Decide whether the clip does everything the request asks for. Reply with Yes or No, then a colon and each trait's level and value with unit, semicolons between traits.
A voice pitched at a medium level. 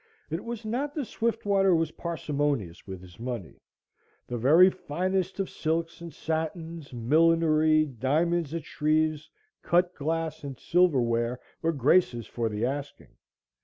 Yes: medium, 155 Hz